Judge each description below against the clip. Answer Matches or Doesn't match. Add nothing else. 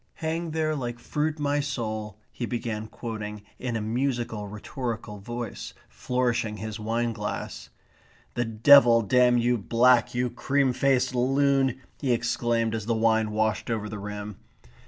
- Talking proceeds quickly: Doesn't match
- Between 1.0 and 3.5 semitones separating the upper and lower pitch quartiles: Matches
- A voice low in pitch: Matches